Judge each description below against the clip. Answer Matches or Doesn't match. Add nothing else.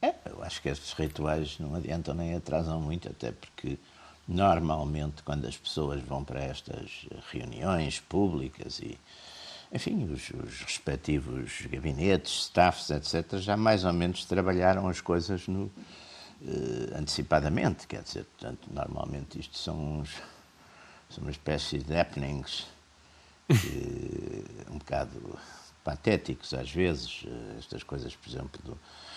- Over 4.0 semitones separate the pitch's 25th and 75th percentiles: Doesn't match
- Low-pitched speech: Matches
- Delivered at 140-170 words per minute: Doesn't match